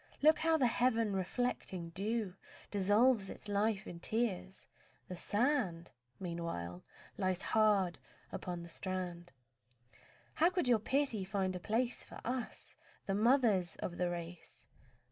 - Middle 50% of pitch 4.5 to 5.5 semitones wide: Yes, average, 4.8 semitones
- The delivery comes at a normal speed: No, slow, 130 wpm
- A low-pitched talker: No, high, 200 Hz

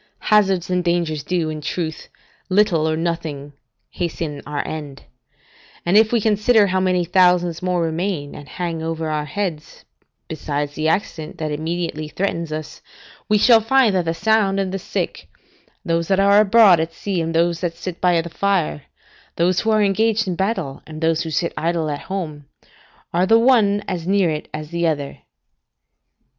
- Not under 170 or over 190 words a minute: Yes, average, 175 wpm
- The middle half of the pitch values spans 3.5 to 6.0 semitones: Yes, average, 3.8 semitones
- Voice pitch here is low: No, medium, 170 Hz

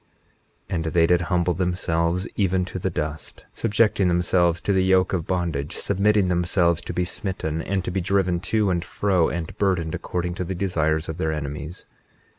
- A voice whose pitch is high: No, very low, 90 Hz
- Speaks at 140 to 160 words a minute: No, average, 185 wpm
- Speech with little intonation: Yes, narrow, 2.1 semitones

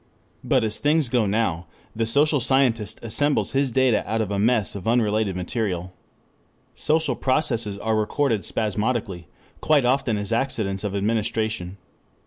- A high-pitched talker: No, low, 110 Hz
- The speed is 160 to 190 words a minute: No, average, 140 wpm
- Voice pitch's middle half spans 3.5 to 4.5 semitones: Yes, average, 4.0 semitones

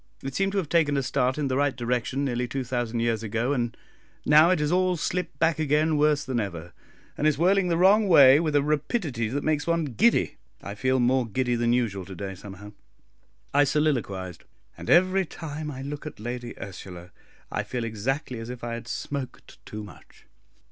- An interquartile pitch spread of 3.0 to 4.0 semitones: No, average, 4.6 semitones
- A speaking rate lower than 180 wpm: No, average, 200 wpm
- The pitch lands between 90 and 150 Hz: Yes, low, 135 Hz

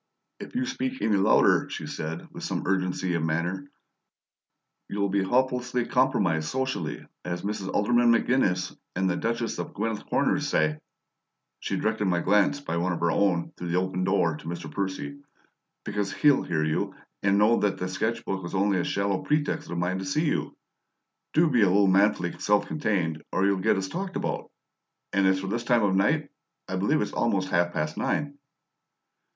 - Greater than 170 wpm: Yes, average, 185 wpm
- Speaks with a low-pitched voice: Yes, very low, 95 Hz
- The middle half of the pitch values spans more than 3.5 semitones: Yes, average, 4.5 semitones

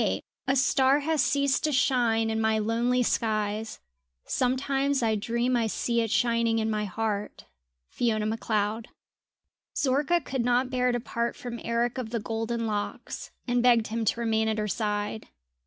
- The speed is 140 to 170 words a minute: Yes, average, 165 wpm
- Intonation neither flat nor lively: No, narrow, 2.2 semitones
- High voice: Yes, high, 235 Hz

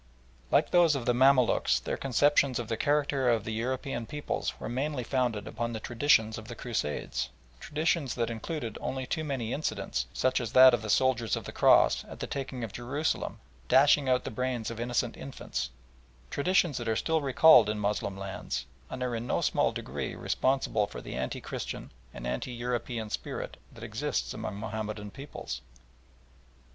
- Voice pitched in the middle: No, low, 120 Hz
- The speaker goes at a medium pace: Yes, average, 175 wpm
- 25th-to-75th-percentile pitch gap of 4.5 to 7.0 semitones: No, average, 3.6 semitones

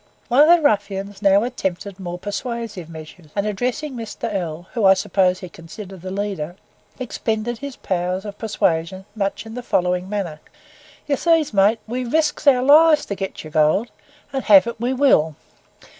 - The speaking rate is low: No, average, 175 wpm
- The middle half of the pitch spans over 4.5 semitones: Yes, average, 5.0 semitones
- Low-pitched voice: No, high, 205 Hz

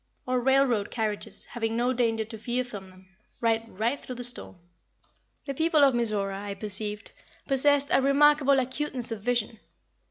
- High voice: Yes, high, 240 Hz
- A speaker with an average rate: Yes, average, 160 wpm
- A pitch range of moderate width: Yes, average, 3.9 semitones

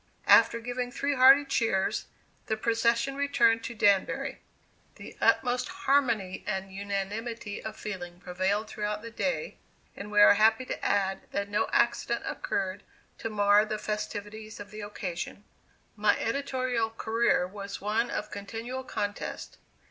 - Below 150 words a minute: Yes, average, 140 wpm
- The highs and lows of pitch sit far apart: No, average, 2.7 semitones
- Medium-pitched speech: No, high, 215 Hz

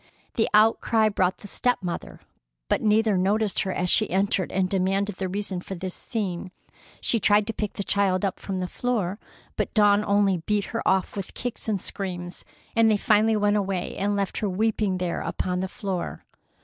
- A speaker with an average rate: Yes, average, 190 wpm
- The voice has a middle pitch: No, high, 200 Hz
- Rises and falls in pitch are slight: Yes, narrow, 2.2 semitones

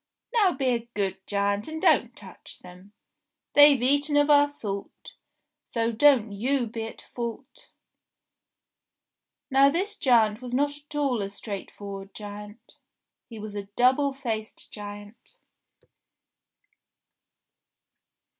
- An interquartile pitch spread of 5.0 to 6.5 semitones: Yes, wide, 5.5 semitones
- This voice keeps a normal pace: No, slow, 120 wpm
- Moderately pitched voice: No, high, 235 Hz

